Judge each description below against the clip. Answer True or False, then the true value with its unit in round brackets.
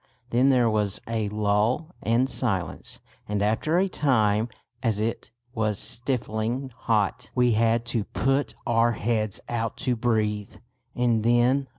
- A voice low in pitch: True (115 Hz)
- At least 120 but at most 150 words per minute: True (140 wpm)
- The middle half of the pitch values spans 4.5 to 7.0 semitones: False (2.5 semitones)